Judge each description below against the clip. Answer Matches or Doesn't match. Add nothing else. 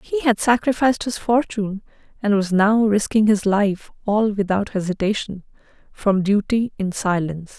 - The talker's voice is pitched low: Doesn't match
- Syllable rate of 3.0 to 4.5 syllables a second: Doesn't match